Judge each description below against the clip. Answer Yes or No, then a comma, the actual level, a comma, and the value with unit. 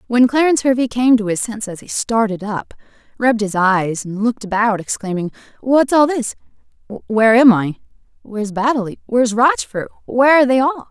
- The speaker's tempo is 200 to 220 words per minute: No, average, 145 wpm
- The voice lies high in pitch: Yes, high, 230 Hz